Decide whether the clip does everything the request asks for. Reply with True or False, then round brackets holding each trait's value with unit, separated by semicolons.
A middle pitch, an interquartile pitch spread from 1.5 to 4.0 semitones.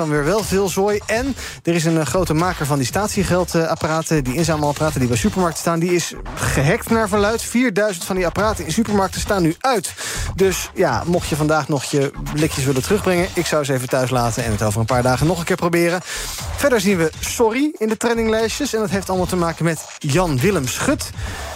False (170 Hz; 5.3 semitones)